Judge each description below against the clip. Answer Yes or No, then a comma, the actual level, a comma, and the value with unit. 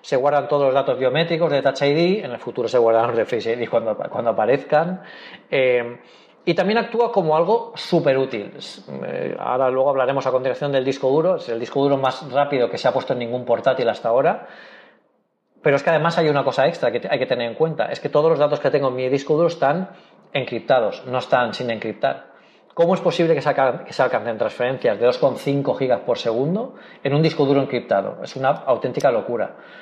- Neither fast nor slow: No, fast, 210 wpm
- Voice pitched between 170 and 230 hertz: No, medium, 140 Hz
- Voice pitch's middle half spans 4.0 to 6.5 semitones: Yes, average, 4.4 semitones